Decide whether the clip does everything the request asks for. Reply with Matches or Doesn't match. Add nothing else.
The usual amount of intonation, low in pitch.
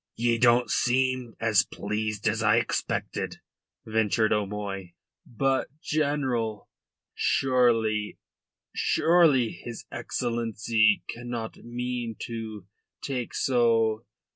Doesn't match